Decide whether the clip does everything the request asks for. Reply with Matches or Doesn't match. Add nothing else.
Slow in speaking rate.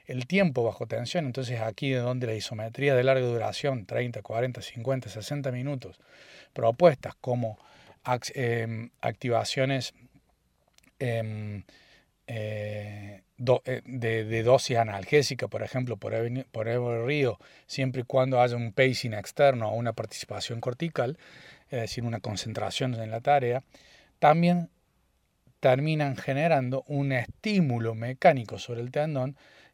Matches